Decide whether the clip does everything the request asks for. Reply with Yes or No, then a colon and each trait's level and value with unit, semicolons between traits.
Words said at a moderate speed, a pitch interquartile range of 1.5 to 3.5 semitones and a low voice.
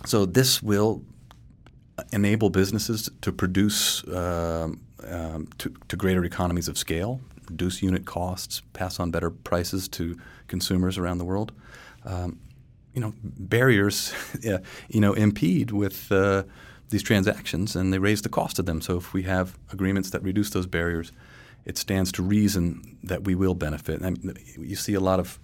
Yes: average, 165 wpm; average, 2.8 semitones; very low, 95 Hz